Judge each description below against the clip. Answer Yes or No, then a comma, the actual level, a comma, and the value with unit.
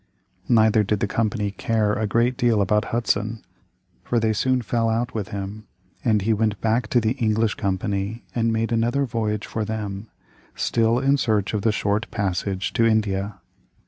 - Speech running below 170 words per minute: No, average, 175 wpm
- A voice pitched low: Yes, low, 110 Hz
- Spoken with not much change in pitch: Yes, narrow, 2.0 semitones